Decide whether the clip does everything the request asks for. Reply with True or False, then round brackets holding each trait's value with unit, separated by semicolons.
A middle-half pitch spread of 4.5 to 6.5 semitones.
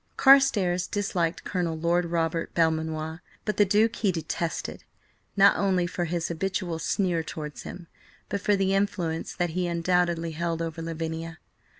False (2.7 semitones)